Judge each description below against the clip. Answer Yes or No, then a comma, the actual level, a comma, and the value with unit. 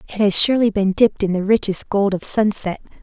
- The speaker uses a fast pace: Yes, fast, 220 wpm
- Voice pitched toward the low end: No, high, 205 Hz